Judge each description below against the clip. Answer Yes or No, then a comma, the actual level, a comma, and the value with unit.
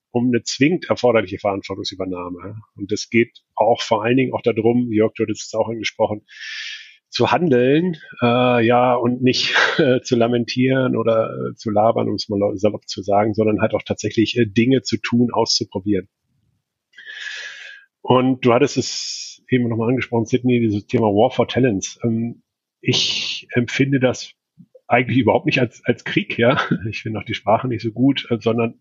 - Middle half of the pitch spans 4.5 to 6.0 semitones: No, average, 2.9 semitones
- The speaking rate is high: No, average, 170 wpm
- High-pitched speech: No, low, 115 Hz